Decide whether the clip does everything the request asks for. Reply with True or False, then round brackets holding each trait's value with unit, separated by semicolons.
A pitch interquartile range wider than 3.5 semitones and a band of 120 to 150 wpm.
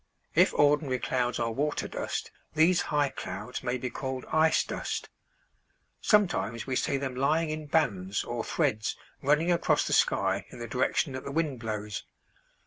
False (4.4 semitones; 160 wpm)